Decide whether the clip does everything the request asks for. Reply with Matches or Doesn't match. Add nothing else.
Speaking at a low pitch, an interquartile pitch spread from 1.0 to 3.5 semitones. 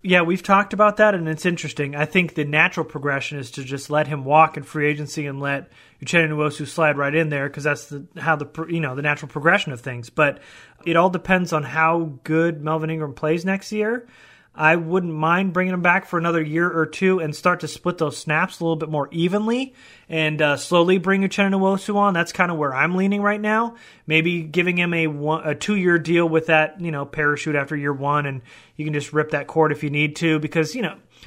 Doesn't match